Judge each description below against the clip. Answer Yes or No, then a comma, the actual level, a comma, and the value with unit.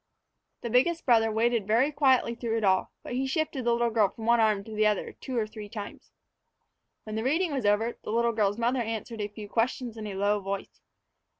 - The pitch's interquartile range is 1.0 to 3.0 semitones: Yes, narrow, 2.5 semitones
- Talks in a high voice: Yes, high, 225 Hz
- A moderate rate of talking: No, fast, 220 wpm